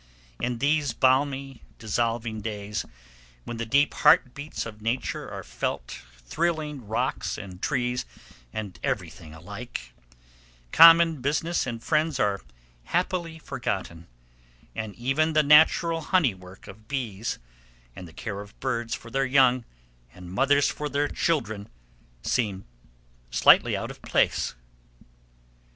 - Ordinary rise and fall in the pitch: No, wide, 5.9 semitones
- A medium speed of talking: No, slow, 125 wpm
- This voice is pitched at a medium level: No, low, 125 Hz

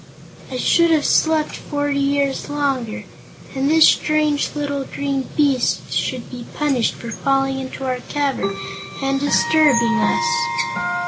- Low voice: No, very high, 275 Hz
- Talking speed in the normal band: No, slow, 130 wpm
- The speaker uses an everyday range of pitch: Yes, average, 3.3 semitones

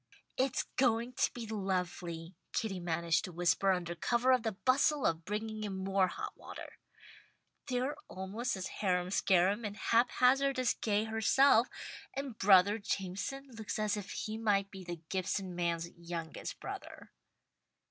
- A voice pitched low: No, high, 200 Hz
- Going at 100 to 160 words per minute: Yes, average, 150 wpm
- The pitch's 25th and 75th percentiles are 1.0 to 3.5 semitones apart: No, average, 4.5 semitones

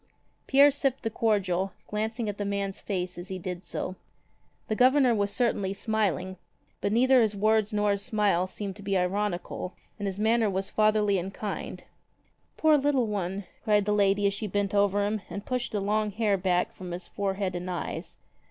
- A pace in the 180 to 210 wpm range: Yes, average, 190 wpm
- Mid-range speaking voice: No, high, 205 Hz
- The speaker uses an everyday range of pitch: No, narrow, 2.2 semitones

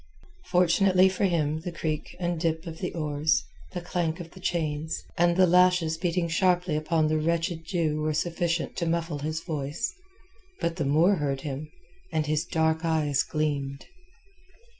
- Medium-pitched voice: Yes, medium, 165 Hz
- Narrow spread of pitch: Yes, narrow, 2.2 semitones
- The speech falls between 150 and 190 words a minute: Yes, average, 160 wpm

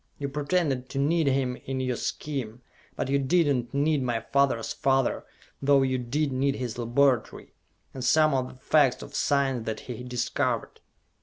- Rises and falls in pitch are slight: Yes, narrow, 2.1 semitones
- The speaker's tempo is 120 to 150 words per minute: No, average, 170 wpm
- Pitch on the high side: No, low, 135 Hz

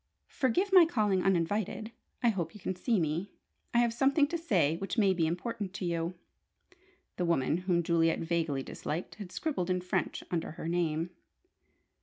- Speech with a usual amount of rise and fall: Yes, average, 4.9 semitones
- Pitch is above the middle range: No, medium, 180 Hz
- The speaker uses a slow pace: No, average, 170 wpm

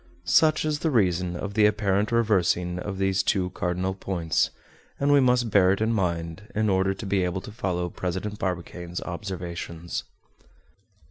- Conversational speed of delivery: Yes, average, 160 wpm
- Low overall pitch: Yes, very low, 95 Hz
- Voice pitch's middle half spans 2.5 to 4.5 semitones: Yes, average, 3.0 semitones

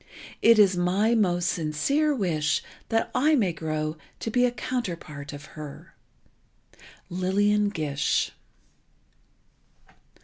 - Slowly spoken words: Yes, slow, 105 wpm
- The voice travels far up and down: Yes, wide, 6.5 semitones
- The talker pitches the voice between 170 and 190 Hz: Yes, medium, 185 Hz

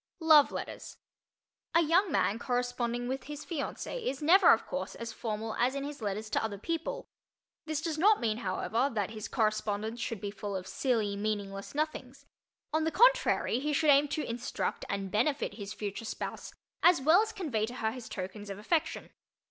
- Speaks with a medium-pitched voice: No, high, 245 Hz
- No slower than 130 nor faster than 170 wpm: No, average, 185 wpm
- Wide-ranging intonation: Yes, wide, 6.2 semitones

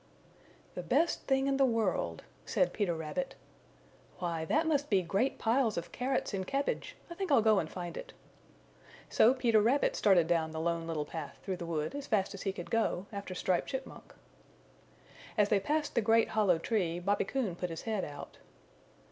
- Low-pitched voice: No, high, 200 Hz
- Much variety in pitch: Yes, wide, 6.6 semitones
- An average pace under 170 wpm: No, average, 190 wpm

